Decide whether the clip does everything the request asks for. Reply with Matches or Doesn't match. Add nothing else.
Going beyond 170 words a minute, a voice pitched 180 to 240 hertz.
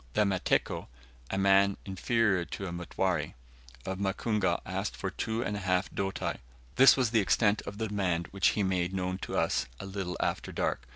Doesn't match